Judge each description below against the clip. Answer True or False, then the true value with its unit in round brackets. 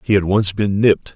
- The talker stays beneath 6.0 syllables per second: True (5.7 syllables/s)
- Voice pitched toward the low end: True (100 Hz)